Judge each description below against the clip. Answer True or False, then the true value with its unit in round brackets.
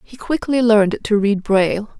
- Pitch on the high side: True (215 Hz)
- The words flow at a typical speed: True (180 wpm)